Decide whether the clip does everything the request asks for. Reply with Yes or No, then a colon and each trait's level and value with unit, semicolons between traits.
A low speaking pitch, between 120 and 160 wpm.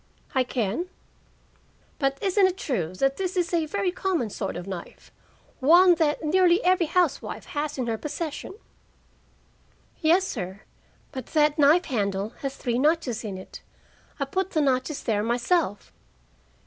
No: very high, 295 Hz; average, 150 wpm